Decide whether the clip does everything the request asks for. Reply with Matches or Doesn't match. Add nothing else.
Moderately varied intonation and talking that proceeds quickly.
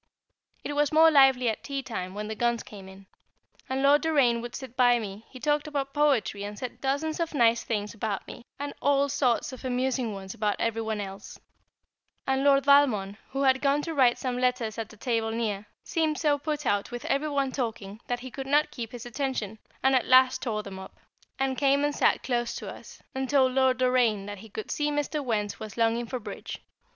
Matches